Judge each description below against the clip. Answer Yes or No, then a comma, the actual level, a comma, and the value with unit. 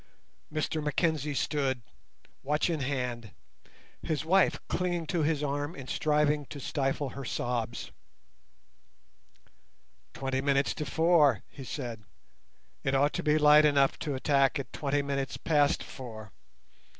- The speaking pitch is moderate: Yes, medium, 145 Hz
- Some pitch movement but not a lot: No, narrow, 2.1 semitones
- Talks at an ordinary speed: No, slow, 130 wpm